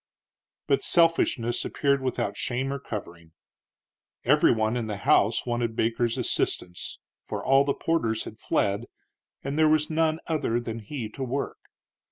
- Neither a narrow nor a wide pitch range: Yes, average, 3.9 semitones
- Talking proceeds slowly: No, average, 150 wpm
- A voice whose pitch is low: Yes, low, 120 Hz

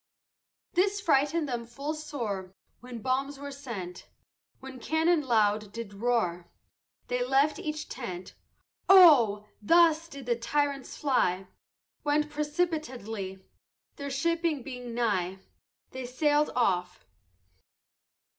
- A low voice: No, very high, 260 Hz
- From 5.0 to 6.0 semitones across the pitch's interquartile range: Yes, wide, 5.4 semitones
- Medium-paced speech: No, slow, 110 wpm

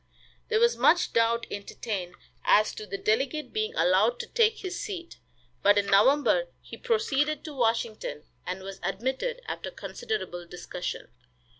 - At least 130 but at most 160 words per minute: Yes, average, 145 wpm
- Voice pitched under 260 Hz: No, very high, 265 Hz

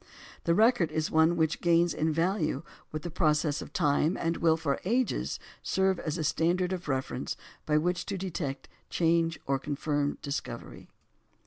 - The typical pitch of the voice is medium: Yes, medium, 165 Hz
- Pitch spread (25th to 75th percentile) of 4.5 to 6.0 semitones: No, narrow, 2.5 semitones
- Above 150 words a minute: Yes, average, 160 wpm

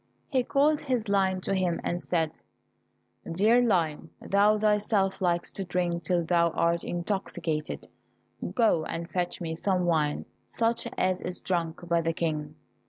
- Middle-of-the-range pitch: Yes, medium, 180 Hz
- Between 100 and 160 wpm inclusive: Yes, average, 150 wpm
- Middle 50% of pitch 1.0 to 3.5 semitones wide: Yes, average, 3.2 semitones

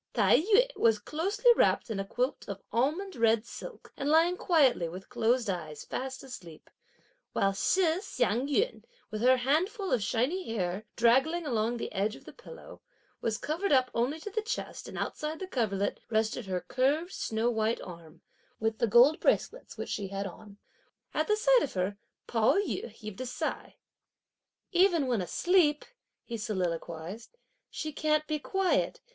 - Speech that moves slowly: No, average, 165 wpm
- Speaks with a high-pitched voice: Yes, high, 245 Hz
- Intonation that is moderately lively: No, wide, 7.3 semitones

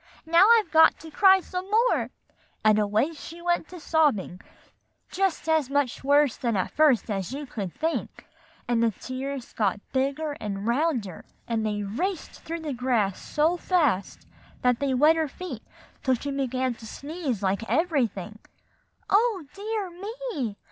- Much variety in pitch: Yes, wide, 6.6 semitones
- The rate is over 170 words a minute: No, average, 155 wpm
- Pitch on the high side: Yes, very high, 280 Hz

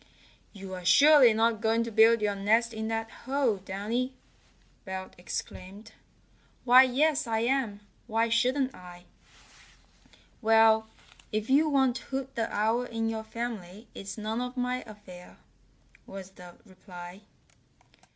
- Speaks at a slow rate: Yes, slow, 130 wpm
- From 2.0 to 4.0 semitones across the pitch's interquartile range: Yes, average, 3.6 semitones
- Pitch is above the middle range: Yes, high, 225 Hz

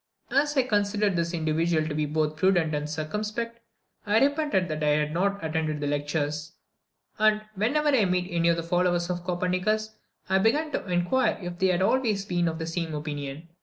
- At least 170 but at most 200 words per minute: Yes, average, 190 wpm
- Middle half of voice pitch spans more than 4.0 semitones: Yes, average, 5.0 semitones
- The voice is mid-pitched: Yes, medium, 175 Hz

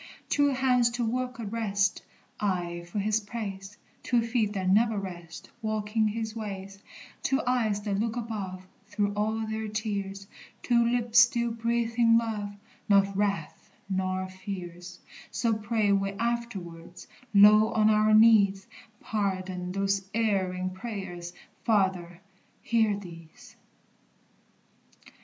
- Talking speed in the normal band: No, slow, 120 wpm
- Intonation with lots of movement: No, average, 2.9 semitones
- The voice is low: No, high, 210 Hz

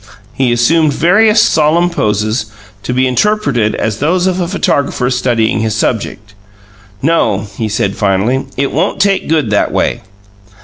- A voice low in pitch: Yes, low, 130 Hz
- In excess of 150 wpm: No, average, 145 wpm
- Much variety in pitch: Yes, wide, 7.3 semitones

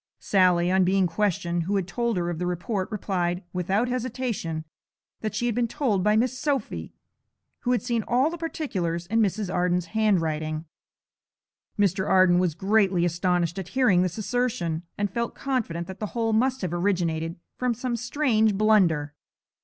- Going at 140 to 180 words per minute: Yes, average, 165 wpm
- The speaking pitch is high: Yes, high, 195 Hz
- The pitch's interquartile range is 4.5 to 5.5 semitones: Yes, average, 4.9 semitones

